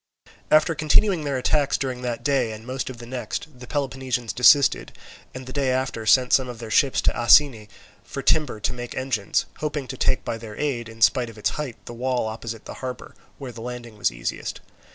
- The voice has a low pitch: Yes, low, 125 Hz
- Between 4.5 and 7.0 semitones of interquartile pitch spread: No, average, 3.0 semitones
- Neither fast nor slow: No, fast, 210 wpm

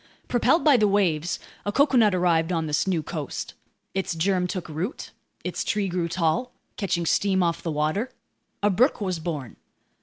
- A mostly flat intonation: No, average, 3.9 semitones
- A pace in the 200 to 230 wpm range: No, average, 170 wpm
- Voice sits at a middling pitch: Yes, medium, 180 Hz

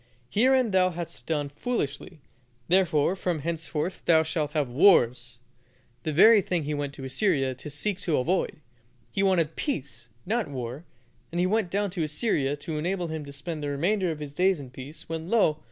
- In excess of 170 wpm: Yes, average, 185 wpm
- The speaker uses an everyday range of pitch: Yes, average, 4.5 semitones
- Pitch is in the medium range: Yes, medium, 160 Hz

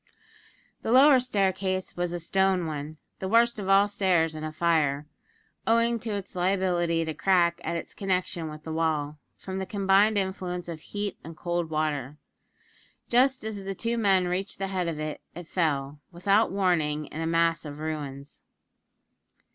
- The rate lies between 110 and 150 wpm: No, average, 170 wpm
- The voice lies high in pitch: No, medium, 180 Hz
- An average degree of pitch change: Yes, average, 3.7 semitones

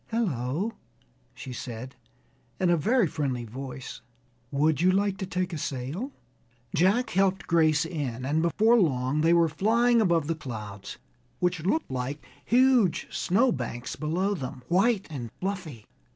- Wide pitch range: Yes, wide, 6.8 semitones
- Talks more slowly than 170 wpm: Yes, average, 145 wpm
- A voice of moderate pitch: Yes, medium, 165 Hz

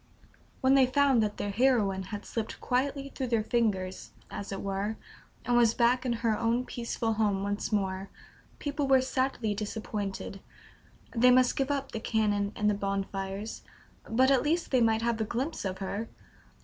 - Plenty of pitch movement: No, average, 4.0 semitones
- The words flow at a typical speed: Yes, average, 175 wpm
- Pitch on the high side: Yes, high, 225 Hz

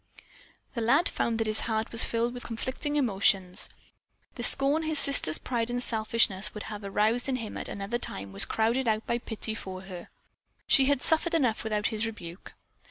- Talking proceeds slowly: No, average, 185 wpm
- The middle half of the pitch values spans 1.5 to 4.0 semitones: Yes, average, 3.0 semitones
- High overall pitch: Yes, high, 225 Hz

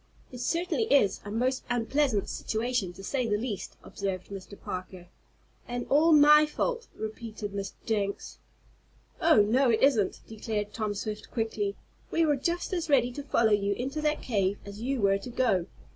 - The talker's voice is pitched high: Yes, high, 230 Hz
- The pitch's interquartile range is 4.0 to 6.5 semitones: Yes, average, 5.3 semitones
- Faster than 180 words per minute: No, average, 170 wpm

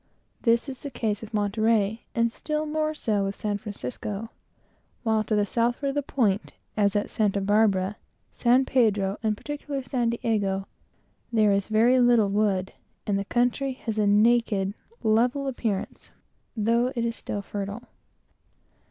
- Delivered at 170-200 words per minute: No, average, 155 wpm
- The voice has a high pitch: Yes, high, 220 Hz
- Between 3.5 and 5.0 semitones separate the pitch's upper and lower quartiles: No, average, 2.9 semitones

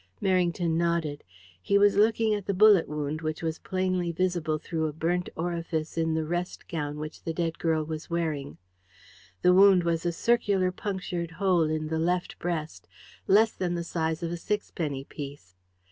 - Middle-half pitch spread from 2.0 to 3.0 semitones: Yes, narrow, 2.5 semitones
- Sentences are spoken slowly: No, average, 175 wpm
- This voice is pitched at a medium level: Yes, medium, 170 Hz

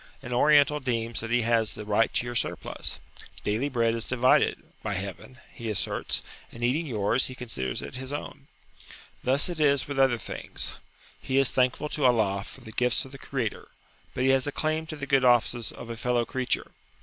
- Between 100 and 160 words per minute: No, average, 200 wpm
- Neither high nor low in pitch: No, low, 125 Hz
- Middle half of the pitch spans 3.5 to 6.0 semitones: No, average, 2.8 semitones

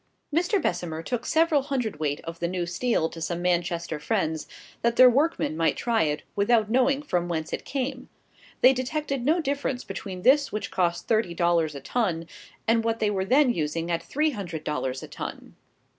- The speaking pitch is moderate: No, high, 205 Hz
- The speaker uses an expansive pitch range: Yes, wide, 7.5 semitones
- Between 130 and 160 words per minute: No, average, 185 wpm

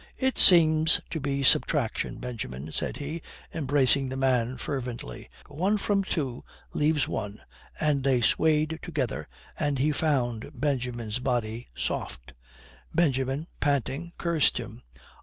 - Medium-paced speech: No, slow, 120 wpm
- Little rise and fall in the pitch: No, average, 4.0 semitones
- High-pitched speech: No, medium, 140 Hz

